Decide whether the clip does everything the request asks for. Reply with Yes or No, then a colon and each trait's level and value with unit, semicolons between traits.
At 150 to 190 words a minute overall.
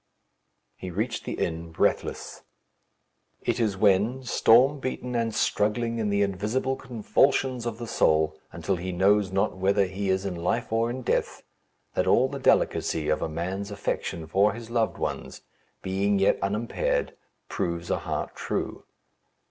Yes: average, 155 wpm